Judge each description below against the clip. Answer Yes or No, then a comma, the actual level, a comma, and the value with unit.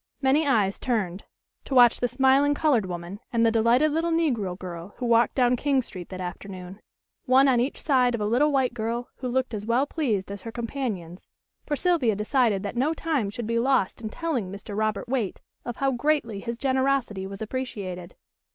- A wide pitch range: No, average, 4.8 semitones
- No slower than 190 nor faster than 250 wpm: Yes, average, 195 wpm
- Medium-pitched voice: No, high, 235 Hz